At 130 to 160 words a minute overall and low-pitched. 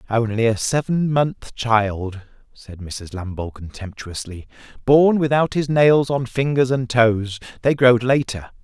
Yes: average, 140 wpm; low, 120 Hz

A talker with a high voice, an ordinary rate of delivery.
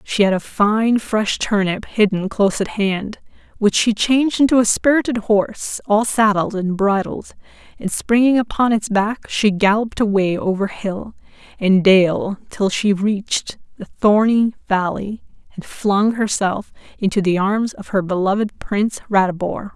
Yes: high, 210 Hz; average, 150 wpm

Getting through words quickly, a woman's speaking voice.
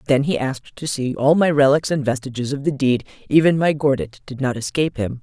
Yes: fast, 230 wpm; female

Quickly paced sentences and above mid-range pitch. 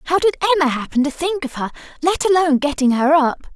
Yes: fast, 220 wpm; very high, 310 Hz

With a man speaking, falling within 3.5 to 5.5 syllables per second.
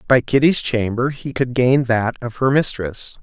Yes: male; 4.3 syllables/s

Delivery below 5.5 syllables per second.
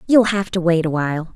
No: 6.0 syllables/s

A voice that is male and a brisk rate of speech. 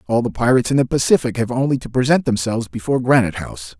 Yes: male; fast, 220 wpm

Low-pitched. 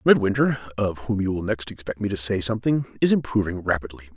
Yes: low, 105 Hz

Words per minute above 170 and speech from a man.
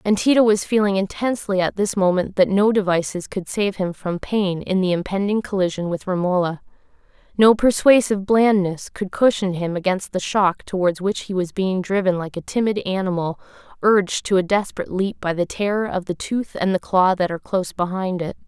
No: average, 195 wpm; female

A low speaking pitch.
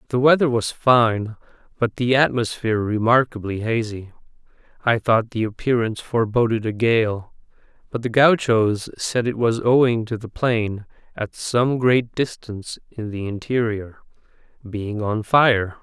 Yes: low, 115 Hz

